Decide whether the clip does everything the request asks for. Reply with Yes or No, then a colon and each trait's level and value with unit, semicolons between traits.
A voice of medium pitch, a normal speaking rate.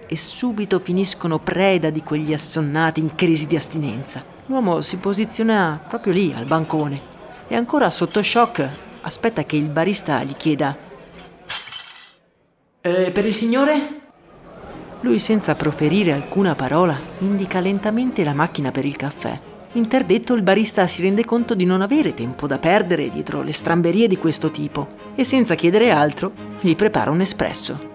Yes: medium, 180 Hz; average, 150 wpm